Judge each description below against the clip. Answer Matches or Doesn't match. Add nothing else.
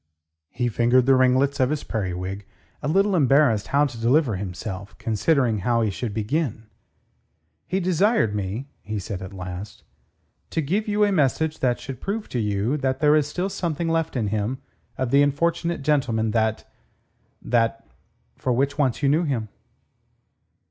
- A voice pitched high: Doesn't match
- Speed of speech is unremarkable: Matches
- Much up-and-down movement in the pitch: Matches